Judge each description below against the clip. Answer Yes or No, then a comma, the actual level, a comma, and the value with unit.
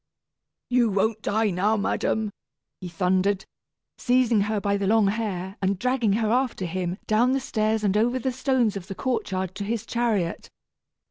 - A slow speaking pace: No, average, 165 wpm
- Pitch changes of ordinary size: Yes, average, 3.3 semitones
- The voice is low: No, high, 215 Hz